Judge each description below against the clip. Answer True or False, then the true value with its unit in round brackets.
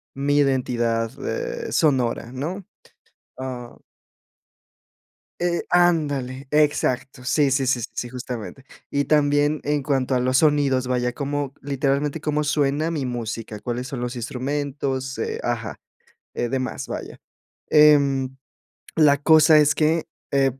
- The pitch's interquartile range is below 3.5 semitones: True (2.7 semitones)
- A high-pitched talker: False (140 Hz)